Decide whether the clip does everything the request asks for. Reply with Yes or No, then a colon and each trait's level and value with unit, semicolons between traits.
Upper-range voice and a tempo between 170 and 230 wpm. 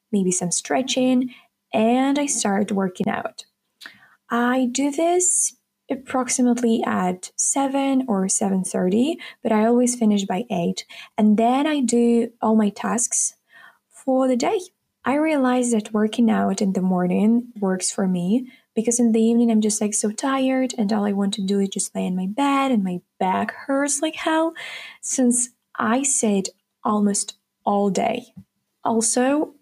No: high, 230 Hz; average, 160 wpm